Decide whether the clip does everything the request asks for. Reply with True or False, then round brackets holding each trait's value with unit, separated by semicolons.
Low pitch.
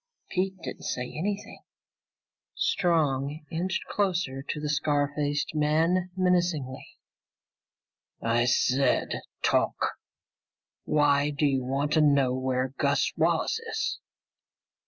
False (145 Hz)